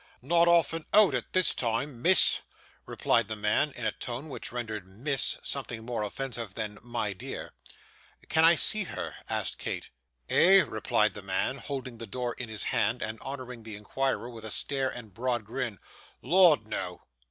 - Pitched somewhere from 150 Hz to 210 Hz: No, low, 120 Hz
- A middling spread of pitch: Yes, average, 4.3 semitones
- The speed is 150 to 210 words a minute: Yes, average, 175 wpm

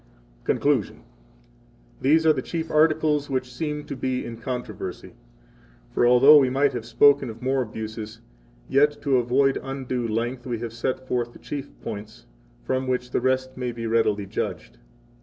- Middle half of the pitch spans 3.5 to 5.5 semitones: No, average, 3.0 semitones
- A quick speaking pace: No, average, 165 wpm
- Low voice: Yes, low, 130 Hz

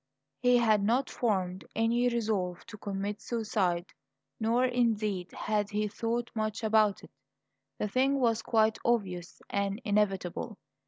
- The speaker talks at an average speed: No, slow, 130 wpm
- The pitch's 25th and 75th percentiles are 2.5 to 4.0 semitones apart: Yes, average, 2.8 semitones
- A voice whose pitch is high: Yes, high, 215 Hz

